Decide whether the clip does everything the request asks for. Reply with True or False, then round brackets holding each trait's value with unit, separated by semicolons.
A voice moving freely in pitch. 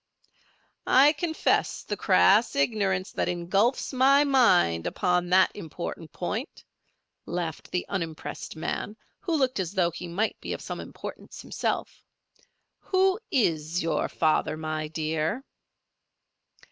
True (7.3 semitones)